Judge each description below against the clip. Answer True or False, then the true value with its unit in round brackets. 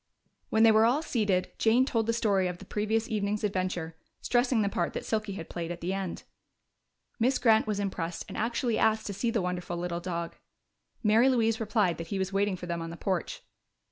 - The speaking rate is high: True (210 wpm)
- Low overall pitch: False (205 Hz)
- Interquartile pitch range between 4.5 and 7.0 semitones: False (3.9 semitones)